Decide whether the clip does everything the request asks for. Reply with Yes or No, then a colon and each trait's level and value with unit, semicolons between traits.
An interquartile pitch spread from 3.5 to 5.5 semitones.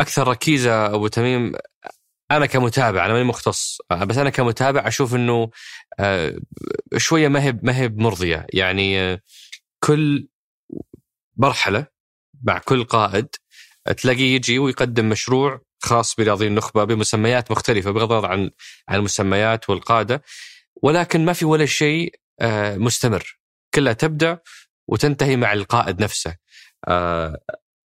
Yes: average, 4.4 semitones